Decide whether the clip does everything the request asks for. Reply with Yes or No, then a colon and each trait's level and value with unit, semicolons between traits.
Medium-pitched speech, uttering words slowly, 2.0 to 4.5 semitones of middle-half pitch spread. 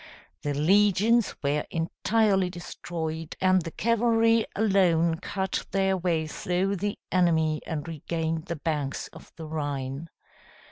Yes: medium, 170 Hz; slow, 125 wpm; average, 3.6 semitones